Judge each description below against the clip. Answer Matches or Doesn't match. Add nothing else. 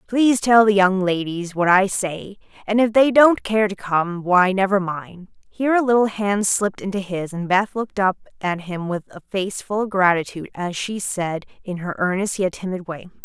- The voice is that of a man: Doesn't match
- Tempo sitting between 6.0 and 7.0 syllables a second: Doesn't match